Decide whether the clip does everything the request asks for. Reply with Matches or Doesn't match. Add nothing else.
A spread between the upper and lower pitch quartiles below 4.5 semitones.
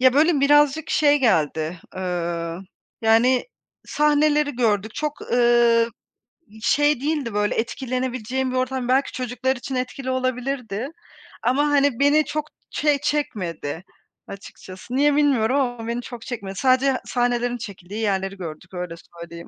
Doesn't match